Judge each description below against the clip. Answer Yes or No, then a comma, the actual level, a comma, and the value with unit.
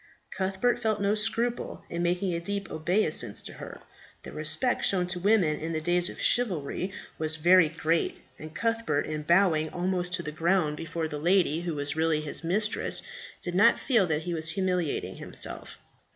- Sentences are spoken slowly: No, average, 180 wpm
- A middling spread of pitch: Yes, average, 3.7 semitones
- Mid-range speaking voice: Yes, medium, 175 Hz